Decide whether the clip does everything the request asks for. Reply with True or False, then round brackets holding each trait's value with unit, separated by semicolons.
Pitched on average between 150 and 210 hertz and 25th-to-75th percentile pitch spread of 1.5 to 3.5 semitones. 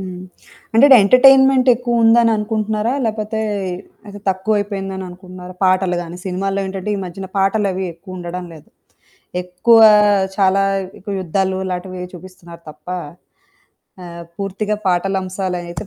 True (190 Hz; 2.7 semitones)